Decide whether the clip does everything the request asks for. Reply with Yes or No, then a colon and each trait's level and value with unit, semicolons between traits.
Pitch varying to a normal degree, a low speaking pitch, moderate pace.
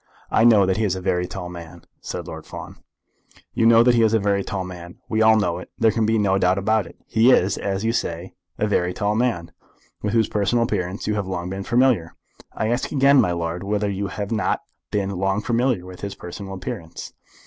No: average, 3.4 semitones; low, 100 Hz; fast, 225 wpm